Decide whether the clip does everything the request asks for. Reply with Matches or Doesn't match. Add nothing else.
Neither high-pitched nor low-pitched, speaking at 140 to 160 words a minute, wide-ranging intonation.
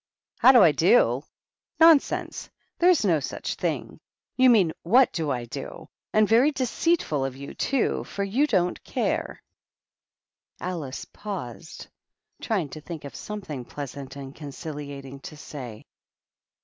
Matches